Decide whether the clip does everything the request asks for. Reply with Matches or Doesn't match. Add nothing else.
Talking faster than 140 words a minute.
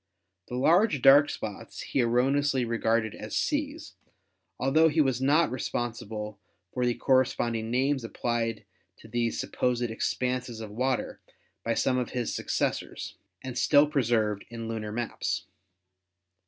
Doesn't match